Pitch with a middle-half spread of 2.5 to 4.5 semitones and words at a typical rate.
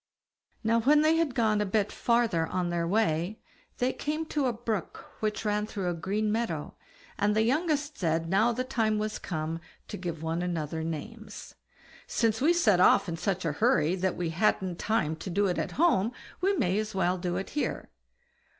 No: average, 5.0 semitones; average, 195 wpm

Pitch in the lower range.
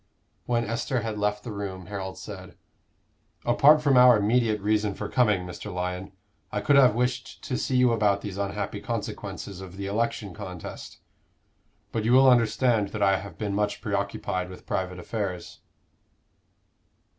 Yes: low, 105 Hz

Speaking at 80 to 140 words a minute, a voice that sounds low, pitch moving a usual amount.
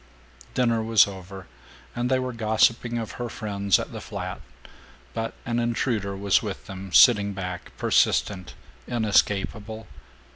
Yes: slow, 135 wpm; low, 110 Hz; average, 3.0 semitones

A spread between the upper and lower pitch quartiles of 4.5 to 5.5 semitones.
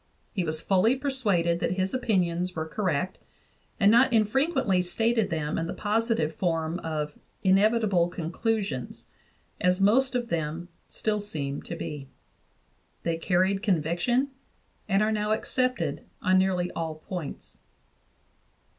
Yes: average, 4.8 semitones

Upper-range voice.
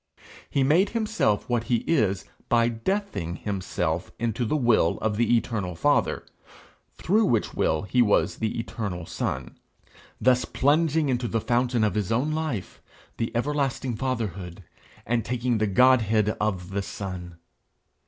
No: low, 115 Hz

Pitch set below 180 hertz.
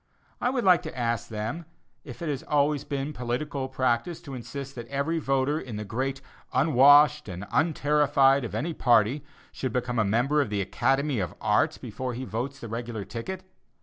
Yes: low, 135 Hz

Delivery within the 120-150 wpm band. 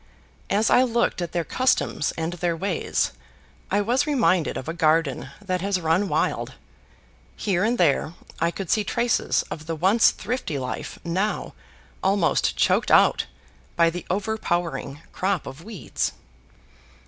Yes: average, 145 wpm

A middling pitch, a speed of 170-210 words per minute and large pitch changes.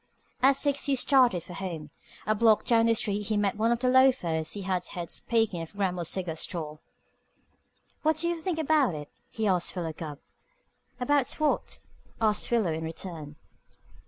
No: high, 205 Hz; average, 175 wpm; wide, 6.8 semitones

